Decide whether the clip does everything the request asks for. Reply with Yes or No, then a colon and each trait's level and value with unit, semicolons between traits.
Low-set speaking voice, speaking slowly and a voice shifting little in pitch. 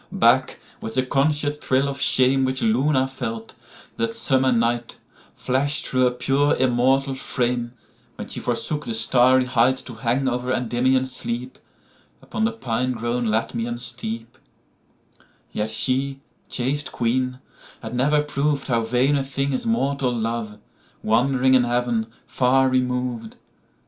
Yes: low, 125 Hz; slow, 120 wpm; narrow, 2.1 semitones